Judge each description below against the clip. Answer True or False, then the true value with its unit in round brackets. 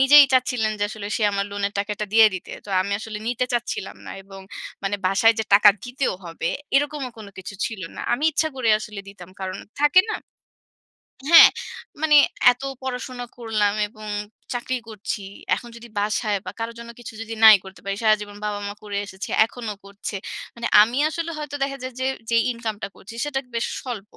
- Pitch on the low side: False (220 Hz)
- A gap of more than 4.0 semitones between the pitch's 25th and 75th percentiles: False (3.5 semitones)